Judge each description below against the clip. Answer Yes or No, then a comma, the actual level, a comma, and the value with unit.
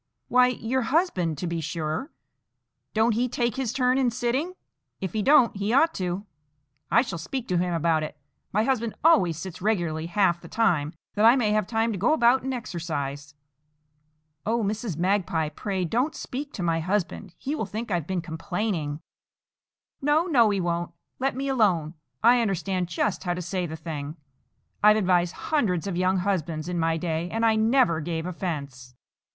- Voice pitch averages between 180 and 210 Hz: Yes, high, 190 Hz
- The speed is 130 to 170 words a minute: No, average, 180 wpm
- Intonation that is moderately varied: No, wide, 5.8 semitones